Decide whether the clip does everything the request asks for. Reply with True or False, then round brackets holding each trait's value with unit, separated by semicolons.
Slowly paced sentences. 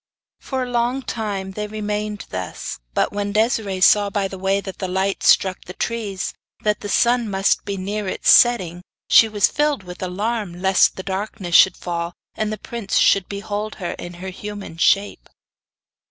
False (180 wpm)